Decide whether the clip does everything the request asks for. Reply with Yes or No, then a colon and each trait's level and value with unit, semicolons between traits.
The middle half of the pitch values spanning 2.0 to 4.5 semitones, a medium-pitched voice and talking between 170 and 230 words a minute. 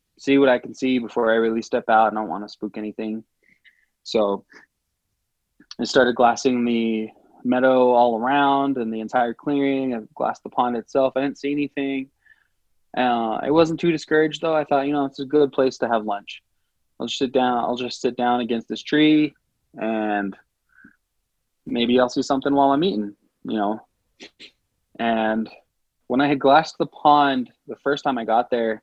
No: average, 3.8 semitones; low, 125 Hz; average, 185 wpm